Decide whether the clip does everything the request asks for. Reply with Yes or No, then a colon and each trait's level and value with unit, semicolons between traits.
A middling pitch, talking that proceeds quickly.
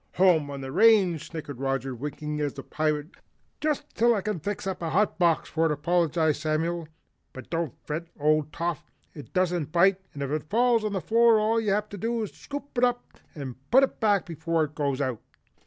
Yes: medium, 170 Hz; fast, 210 wpm